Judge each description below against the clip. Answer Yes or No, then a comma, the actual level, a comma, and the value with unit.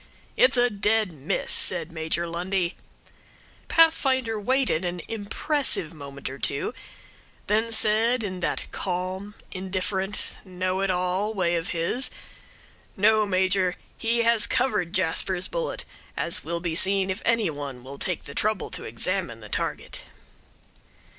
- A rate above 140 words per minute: No, slow, 135 wpm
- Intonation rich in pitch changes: No, average, 4.2 semitones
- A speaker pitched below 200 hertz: Yes, high, 190 Hz